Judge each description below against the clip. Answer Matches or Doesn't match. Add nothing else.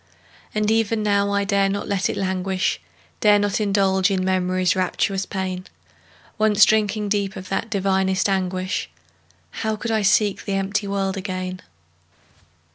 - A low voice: Doesn't match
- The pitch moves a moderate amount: Doesn't match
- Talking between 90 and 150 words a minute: Matches